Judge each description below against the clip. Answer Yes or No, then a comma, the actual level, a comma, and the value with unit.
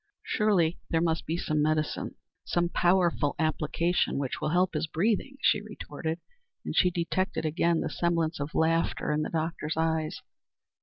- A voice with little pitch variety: Yes, narrow, 2.0 semitones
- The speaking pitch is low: No, medium, 165 Hz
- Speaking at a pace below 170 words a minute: Yes, average, 155 wpm